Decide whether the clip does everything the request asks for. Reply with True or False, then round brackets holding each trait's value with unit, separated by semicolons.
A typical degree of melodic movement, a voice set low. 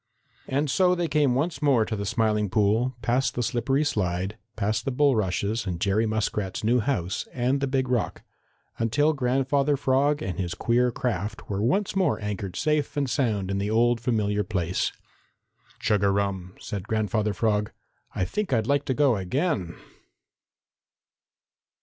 True (5.0 semitones; 115 Hz)